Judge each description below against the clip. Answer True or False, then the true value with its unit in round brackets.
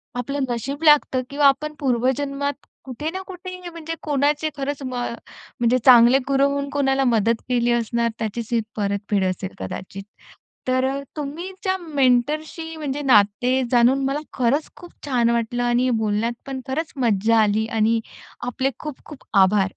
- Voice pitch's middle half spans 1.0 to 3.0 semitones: False (3.8 semitones)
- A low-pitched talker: False (260 Hz)